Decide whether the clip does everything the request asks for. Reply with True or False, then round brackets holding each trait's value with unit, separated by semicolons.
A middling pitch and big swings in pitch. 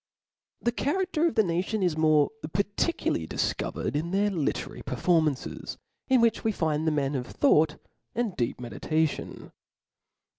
True (170 Hz; 6.6 semitones)